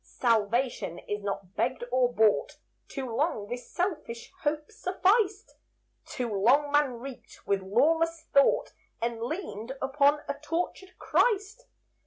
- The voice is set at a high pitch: Yes, very high, 270 Hz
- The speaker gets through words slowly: Yes, slow, 125 wpm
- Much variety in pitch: Yes, wide, 6.1 semitones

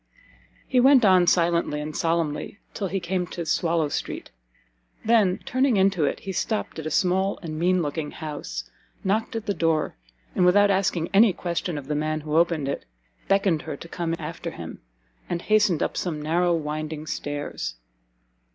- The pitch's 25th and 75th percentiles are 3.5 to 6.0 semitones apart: Yes, average, 3.8 semitones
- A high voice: No, medium, 170 Hz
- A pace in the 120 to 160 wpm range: No, average, 170 wpm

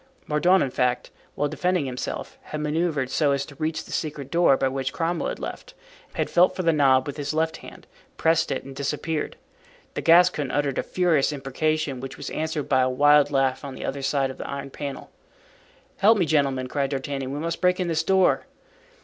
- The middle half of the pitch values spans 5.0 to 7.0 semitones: No, average, 3.1 semitones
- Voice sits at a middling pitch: Yes, medium, 145 Hz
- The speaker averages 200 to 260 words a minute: Yes, fast, 205 wpm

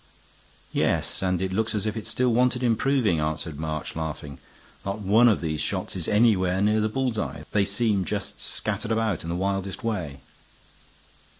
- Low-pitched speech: Yes, low, 100 Hz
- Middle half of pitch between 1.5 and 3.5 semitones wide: No, average, 4.2 semitones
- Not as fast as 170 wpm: No, average, 175 wpm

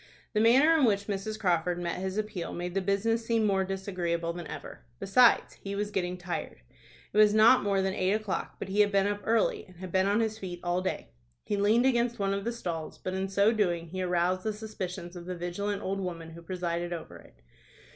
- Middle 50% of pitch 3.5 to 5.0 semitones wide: No, average, 3.1 semitones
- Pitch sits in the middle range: No, high, 195 Hz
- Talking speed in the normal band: No, fast, 225 wpm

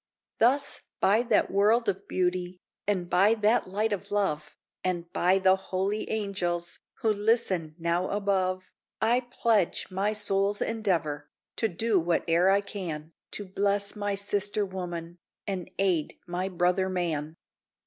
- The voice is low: No, high, 190 Hz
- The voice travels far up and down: No, average, 2.7 semitones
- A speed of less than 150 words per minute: Yes, average, 140 wpm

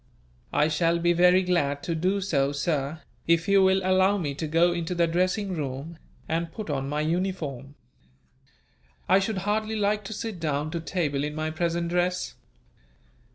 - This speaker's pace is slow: No, average, 170 wpm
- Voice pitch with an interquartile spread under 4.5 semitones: Yes, average, 3.6 semitones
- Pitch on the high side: No, medium, 170 Hz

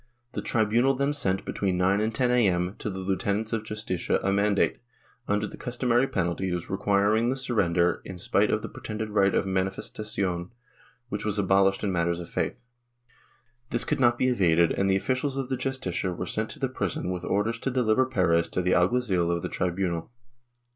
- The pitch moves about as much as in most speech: Yes, average, 4.4 semitones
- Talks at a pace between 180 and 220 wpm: Yes, average, 195 wpm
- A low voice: Yes, low, 100 Hz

